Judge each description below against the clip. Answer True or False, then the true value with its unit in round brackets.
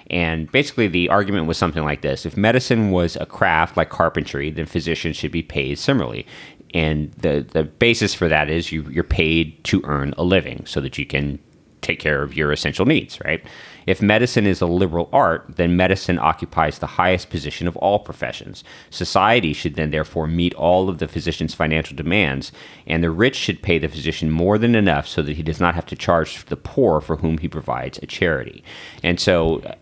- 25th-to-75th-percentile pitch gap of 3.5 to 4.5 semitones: False (3.0 semitones)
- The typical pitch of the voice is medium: False (85 Hz)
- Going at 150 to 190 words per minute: False (200 wpm)